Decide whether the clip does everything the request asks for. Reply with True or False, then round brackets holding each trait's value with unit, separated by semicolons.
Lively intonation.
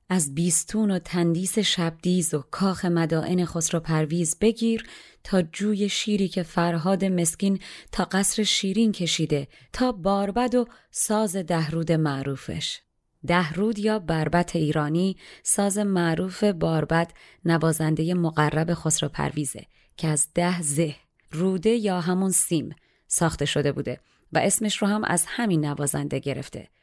False (3.5 semitones)